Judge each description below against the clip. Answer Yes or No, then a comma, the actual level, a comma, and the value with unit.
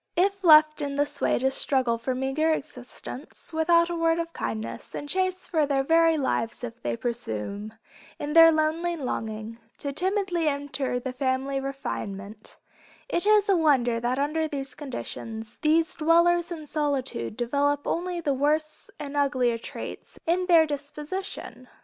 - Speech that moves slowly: No, average, 155 wpm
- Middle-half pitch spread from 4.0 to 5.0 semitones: Yes, average, 4.6 semitones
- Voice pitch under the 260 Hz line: No, very high, 290 Hz